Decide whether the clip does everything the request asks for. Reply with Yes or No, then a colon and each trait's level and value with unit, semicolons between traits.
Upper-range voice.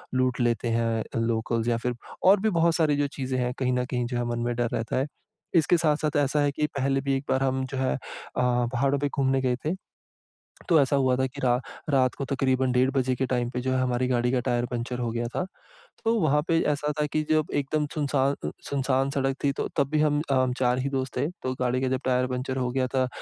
No: low, 130 Hz